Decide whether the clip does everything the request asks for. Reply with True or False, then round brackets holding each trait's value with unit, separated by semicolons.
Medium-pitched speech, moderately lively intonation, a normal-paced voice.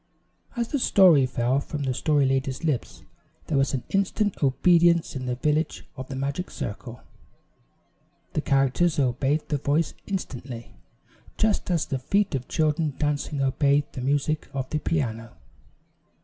True (145 Hz; 3.6 semitones; 145 wpm)